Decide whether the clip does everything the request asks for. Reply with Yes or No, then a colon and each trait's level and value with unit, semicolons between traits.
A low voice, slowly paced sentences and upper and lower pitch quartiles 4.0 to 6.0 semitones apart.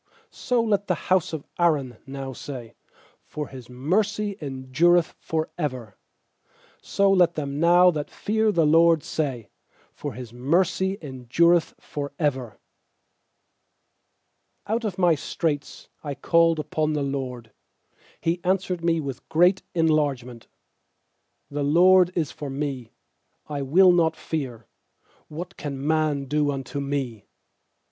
No: medium, 150 Hz; slow, 130 wpm; average, 4.3 semitones